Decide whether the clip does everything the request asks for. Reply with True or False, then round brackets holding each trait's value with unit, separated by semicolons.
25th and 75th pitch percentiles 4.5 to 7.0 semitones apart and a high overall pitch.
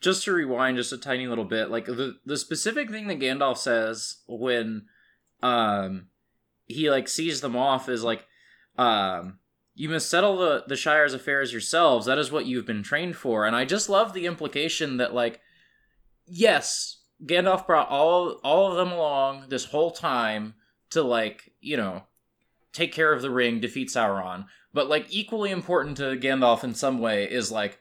False (5.5 semitones; 135 Hz)